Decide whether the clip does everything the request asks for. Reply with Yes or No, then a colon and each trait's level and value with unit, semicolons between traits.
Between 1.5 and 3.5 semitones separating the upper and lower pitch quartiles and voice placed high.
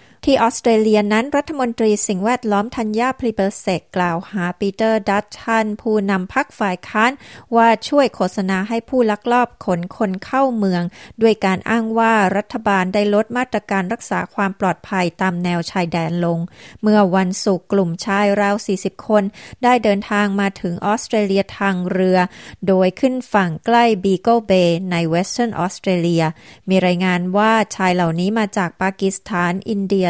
Yes: average, 3.1 semitones; high, 200 Hz